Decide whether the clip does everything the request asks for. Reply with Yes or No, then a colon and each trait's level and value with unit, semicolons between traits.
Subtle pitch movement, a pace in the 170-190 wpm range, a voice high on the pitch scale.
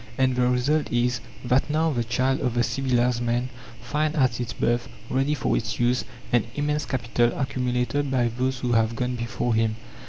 No: narrow, 1.8 semitones; average, 185 wpm; low, 125 Hz